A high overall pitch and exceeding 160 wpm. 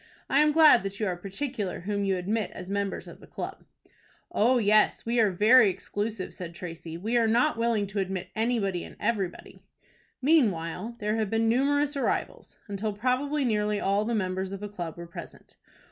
Yes: high, 210 Hz; average, 185 wpm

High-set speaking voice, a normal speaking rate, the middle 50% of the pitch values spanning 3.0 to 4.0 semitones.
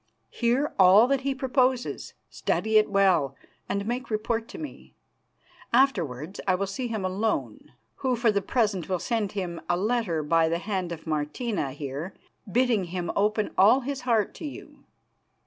No: high, 210 Hz; average, 165 wpm; average, 5.2 semitones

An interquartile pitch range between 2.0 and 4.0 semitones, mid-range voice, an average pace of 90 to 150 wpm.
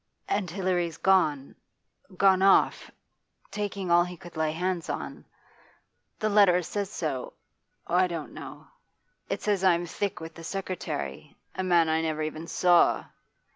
Yes: average, 2.8 semitones; medium, 175 Hz; average, 140 wpm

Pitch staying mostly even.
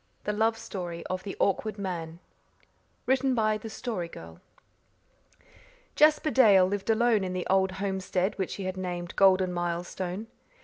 No: average, 3.2 semitones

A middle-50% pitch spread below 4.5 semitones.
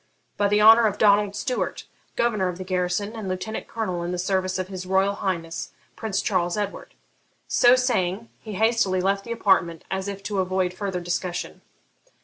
Yes: narrow, 2.4 semitones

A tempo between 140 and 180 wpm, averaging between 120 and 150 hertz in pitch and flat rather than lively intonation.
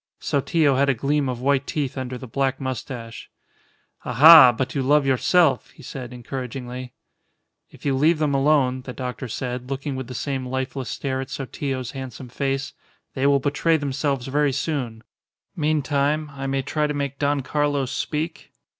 Yes: average, 165 wpm; low, 135 Hz; narrow, 2.0 semitones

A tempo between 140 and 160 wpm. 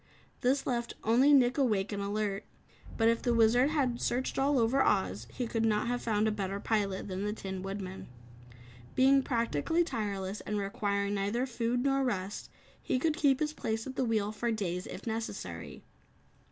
No: average, 180 wpm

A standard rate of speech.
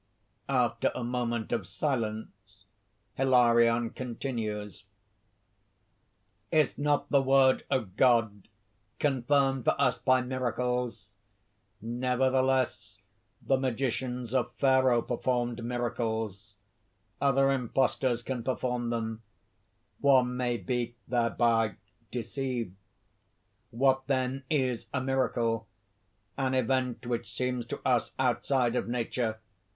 No: slow, 105 wpm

